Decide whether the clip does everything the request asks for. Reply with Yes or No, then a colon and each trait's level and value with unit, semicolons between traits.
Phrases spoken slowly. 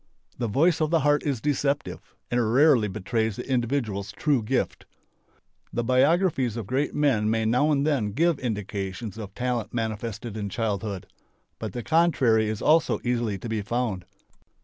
No: average, 160 wpm